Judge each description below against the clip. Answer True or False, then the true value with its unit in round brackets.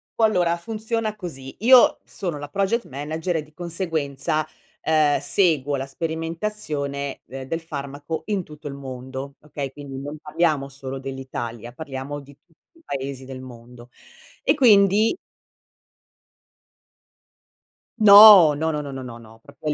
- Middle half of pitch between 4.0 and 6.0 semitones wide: True (4.4 semitones)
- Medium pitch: True (150 Hz)